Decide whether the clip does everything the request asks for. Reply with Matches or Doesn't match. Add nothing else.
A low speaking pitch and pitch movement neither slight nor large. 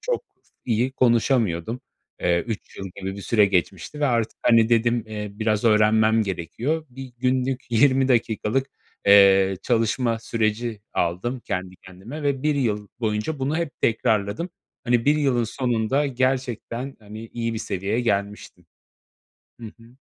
Matches